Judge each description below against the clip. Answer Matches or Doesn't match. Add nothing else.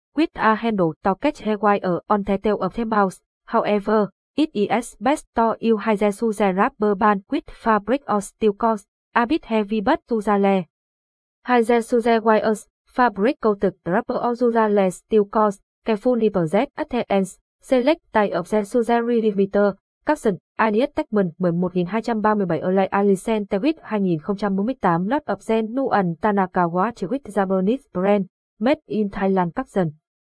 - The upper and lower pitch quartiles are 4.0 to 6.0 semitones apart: Doesn't match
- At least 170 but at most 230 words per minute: Doesn't match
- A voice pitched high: Matches